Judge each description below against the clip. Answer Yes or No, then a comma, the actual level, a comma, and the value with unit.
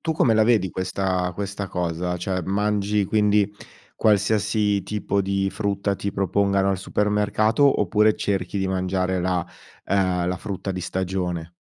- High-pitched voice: No, low, 100 Hz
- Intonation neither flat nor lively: No, narrow, 2.0 semitones